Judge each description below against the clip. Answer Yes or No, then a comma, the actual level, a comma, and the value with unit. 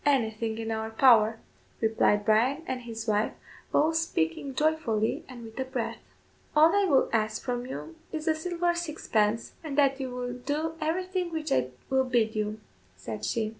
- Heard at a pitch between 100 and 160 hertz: No, very high, 250 Hz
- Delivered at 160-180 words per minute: Yes, average, 170 wpm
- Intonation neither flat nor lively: No, wide, 5.9 semitones